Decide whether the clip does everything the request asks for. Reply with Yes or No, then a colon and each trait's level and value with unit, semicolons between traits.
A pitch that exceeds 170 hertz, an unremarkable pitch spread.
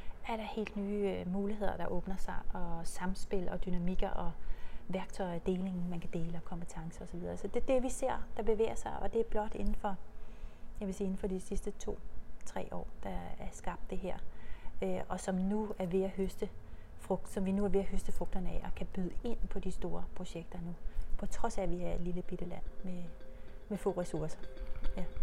No: high, 190 Hz; narrow, 2.3 semitones